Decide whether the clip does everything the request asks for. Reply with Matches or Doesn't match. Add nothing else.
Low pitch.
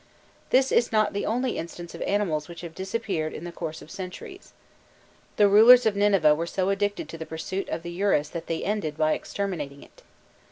Doesn't match